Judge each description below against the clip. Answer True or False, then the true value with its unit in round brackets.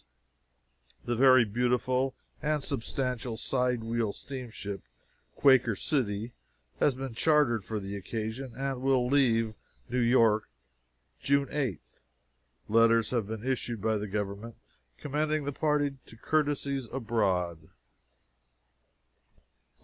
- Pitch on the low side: True (120 Hz)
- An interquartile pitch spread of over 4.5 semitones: False (3.4 semitones)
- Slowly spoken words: True (110 wpm)